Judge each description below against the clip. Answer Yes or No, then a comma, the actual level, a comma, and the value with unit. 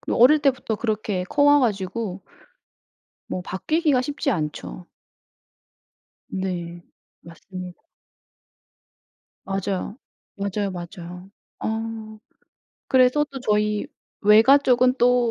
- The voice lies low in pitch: No, high, 215 Hz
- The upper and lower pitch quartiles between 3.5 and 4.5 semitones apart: No, average, 5.1 semitones